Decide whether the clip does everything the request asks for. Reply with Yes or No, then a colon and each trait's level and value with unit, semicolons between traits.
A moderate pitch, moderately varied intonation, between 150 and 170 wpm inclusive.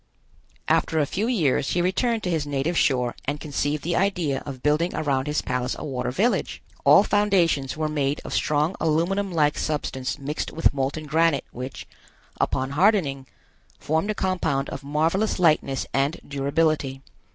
Yes: medium, 150 Hz; average, 4.0 semitones; average, 160 wpm